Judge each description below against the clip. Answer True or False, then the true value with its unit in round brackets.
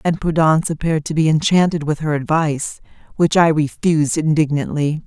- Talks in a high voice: False (155 Hz)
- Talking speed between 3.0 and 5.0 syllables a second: False (5.7 syllables/s)